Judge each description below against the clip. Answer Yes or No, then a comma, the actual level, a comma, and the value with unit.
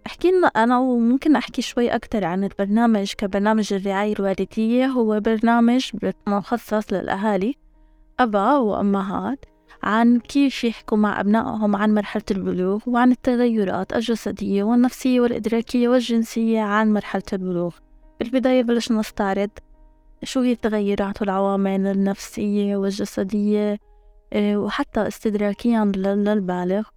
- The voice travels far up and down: No, average, 3.1 semitones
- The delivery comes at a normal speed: Yes, average, 100 wpm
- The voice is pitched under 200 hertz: No, high, 215 Hz